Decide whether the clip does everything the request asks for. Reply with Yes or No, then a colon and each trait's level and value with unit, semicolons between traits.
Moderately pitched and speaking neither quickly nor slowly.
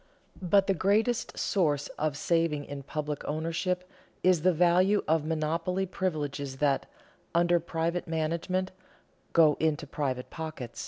No: medium, 165 Hz; slow, 125 wpm